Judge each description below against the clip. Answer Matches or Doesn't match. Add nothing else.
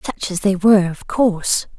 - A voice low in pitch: Doesn't match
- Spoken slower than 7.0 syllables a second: Matches